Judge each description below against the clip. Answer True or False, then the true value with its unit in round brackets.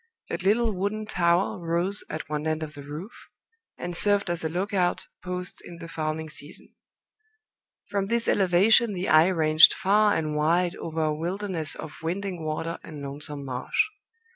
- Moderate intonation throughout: True (3.9 semitones)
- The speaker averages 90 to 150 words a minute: False (165 wpm)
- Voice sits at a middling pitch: True (170 Hz)